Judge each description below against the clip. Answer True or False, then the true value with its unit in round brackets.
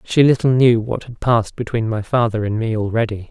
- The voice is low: True (115 Hz)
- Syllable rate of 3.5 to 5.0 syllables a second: False (5.6 syllables/s)